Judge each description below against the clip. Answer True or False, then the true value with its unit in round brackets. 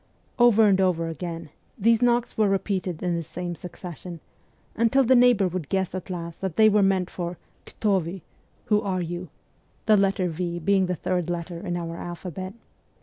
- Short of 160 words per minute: False (195 wpm)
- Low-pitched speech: False (185 Hz)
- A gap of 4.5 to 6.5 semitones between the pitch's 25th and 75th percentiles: False (2.7 semitones)